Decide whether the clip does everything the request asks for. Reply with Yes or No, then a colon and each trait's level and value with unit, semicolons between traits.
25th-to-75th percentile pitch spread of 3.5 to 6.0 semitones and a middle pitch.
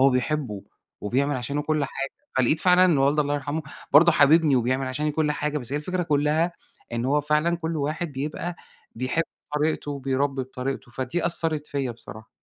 No: average, 2.8 semitones; medium, 145 Hz